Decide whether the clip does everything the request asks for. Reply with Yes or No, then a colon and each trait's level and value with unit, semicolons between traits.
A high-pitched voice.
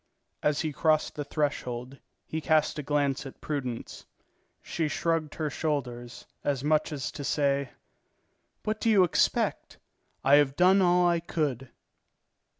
No: medium, 150 Hz